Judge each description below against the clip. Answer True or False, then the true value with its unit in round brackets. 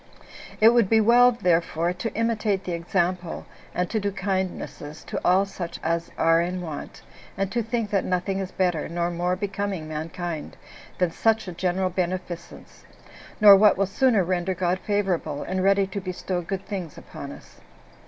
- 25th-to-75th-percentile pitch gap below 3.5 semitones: True (2.5 semitones)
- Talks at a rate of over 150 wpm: True (170 wpm)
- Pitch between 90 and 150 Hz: False (185 Hz)